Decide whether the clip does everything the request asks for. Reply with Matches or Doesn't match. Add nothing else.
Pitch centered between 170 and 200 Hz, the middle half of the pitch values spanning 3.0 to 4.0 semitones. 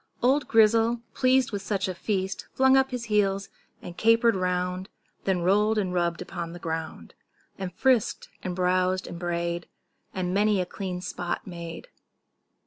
Matches